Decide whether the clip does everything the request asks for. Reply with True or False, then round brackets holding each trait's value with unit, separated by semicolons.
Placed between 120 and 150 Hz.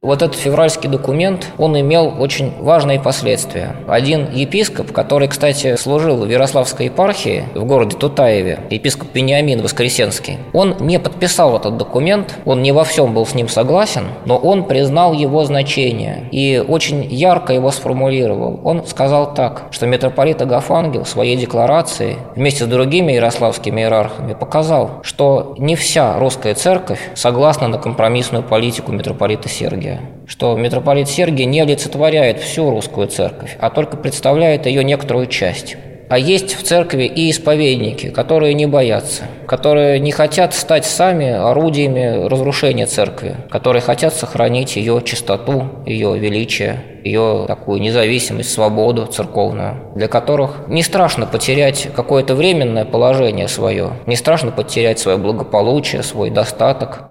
True (135 Hz)